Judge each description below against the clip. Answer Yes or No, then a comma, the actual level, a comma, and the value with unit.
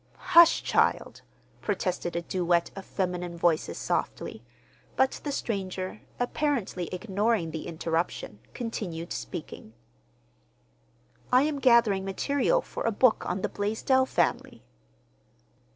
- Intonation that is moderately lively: No, wide, 6.2 semitones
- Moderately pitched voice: No, high, 195 Hz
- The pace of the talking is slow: Yes, slow, 110 wpm